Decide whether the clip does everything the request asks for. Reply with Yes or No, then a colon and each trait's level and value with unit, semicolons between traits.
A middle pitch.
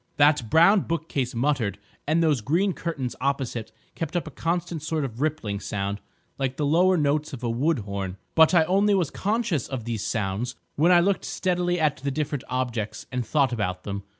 Yes: medium, 145 Hz